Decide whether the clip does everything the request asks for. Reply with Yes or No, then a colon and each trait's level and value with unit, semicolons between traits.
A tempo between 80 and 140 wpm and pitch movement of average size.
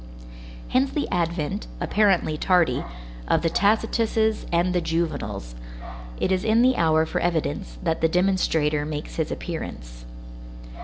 Yes: slow, 135 wpm; average, 4.1 semitones